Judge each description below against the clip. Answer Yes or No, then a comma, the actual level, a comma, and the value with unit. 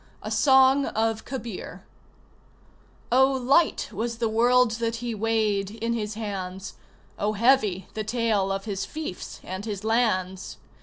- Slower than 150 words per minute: Yes, average, 140 wpm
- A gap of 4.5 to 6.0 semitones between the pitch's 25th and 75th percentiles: No, average, 3.2 semitones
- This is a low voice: No, high, 225 Hz